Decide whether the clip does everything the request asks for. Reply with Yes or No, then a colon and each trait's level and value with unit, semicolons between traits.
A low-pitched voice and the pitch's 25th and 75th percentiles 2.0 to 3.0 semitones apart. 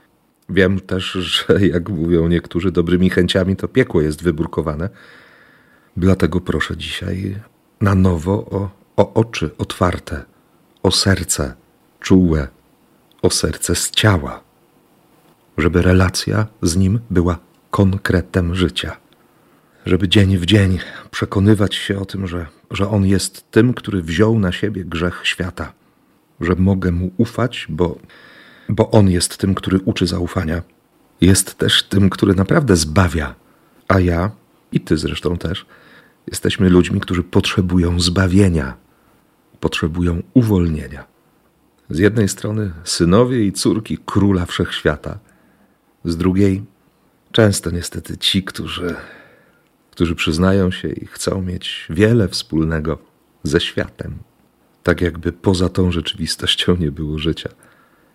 Yes: very low, 95 Hz; narrow, 2.4 semitones